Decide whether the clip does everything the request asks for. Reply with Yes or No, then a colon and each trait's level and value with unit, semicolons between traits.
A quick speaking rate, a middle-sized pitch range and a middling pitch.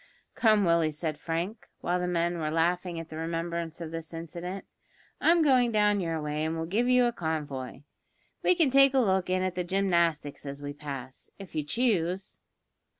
No: average, 190 wpm; average, 3.7 semitones; medium, 170 Hz